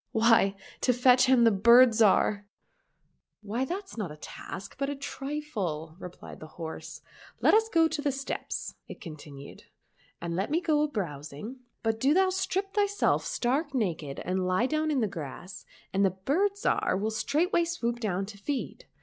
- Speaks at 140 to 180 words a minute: No, average, 190 wpm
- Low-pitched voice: No, high, 235 Hz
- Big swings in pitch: Yes, wide, 7.9 semitones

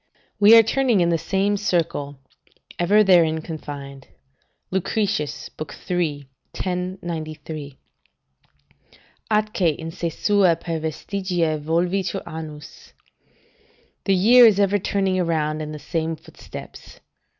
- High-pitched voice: No, medium, 170 Hz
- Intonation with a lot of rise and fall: No, average, 4.0 semitones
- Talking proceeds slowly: Yes, slow, 105 wpm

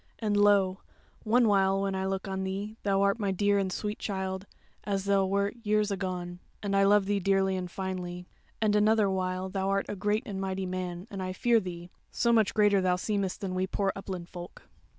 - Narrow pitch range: Yes, narrow, 1.6 semitones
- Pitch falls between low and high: No, high, 195 Hz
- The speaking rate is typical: No, fast, 210 wpm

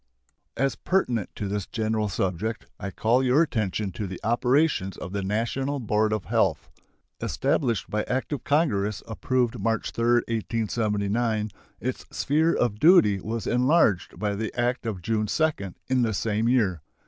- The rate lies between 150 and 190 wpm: Yes, average, 155 wpm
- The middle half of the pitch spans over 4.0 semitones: No, average, 3.5 semitones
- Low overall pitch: Yes, low, 110 Hz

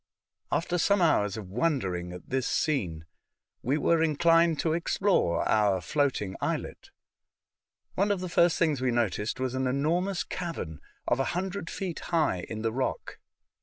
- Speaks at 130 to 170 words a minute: Yes, average, 155 wpm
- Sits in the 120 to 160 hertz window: Yes, medium, 140 Hz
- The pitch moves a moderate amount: No, wide, 7.9 semitones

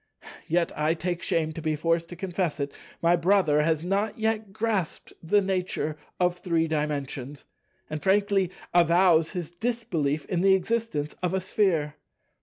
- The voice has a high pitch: No, medium, 175 Hz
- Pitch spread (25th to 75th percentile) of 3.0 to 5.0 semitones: Yes, average, 3.6 semitones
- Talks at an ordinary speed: Yes, average, 145 wpm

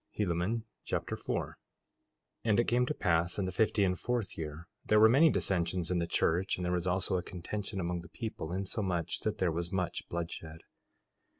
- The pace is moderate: Yes, average, 195 wpm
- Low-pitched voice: Yes, very low, 90 Hz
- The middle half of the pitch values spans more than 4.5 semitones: No, average, 3.6 semitones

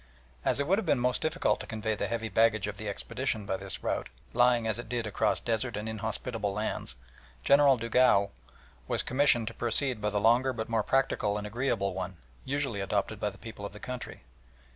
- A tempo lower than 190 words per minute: No, fast, 205 wpm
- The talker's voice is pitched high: No, low, 115 Hz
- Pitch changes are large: No, average, 3.3 semitones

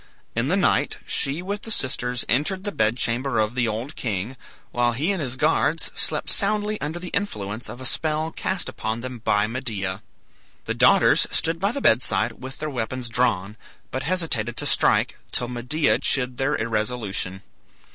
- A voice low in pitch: Yes, low, 125 Hz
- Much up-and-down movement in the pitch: Yes, wide, 5.8 semitones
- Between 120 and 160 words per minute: No, average, 175 wpm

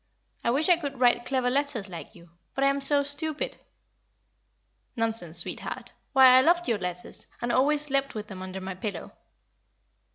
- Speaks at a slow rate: No, average, 170 wpm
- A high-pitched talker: Yes, very high, 255 Hz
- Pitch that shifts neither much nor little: No, wide, 6.4 semitones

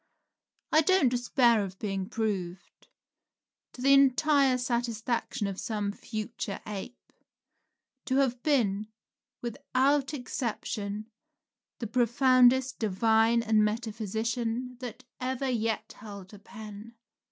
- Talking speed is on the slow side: Yes, slow, 105 wpm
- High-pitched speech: Yes, high, 230 Hz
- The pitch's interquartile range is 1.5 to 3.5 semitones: Yes, average, 3.2 semitones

